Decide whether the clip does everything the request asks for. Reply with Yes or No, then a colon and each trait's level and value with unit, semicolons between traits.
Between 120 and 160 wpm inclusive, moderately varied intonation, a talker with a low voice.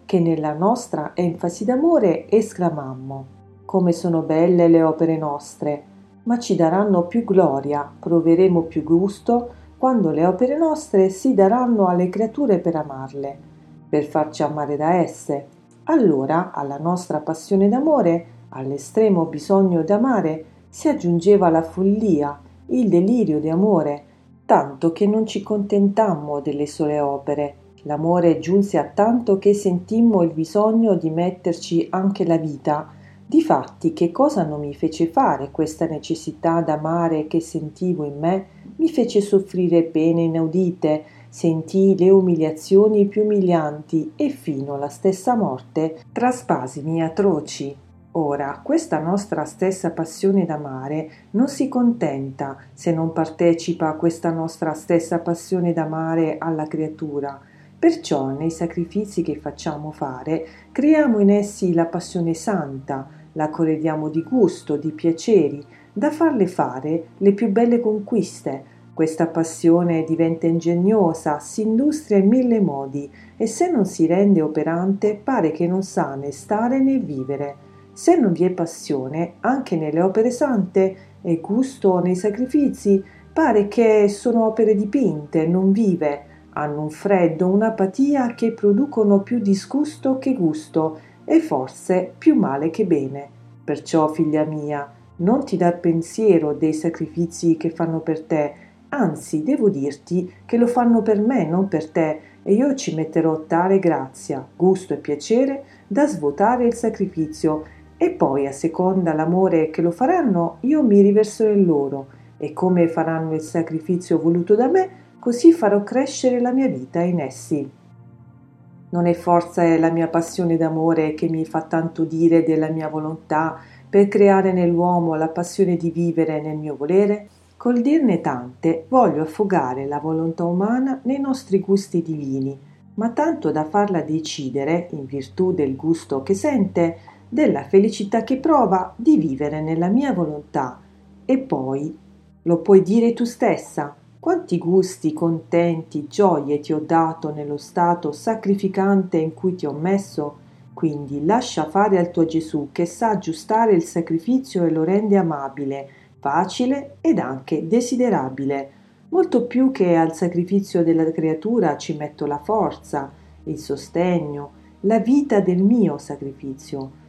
No: average, 140 wpm; average, 4.8 semitones; medium, 170 Hz